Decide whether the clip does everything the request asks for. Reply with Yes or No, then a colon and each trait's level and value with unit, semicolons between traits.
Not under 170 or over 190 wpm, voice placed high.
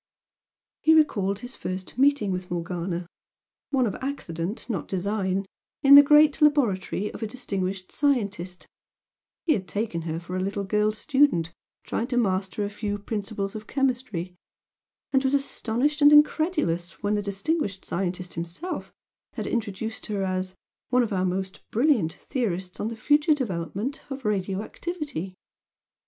No: average, 145 wpm; high, 205 Hz